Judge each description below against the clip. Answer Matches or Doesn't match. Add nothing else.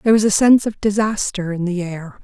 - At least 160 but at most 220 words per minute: Doesn't match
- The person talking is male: Doesn't match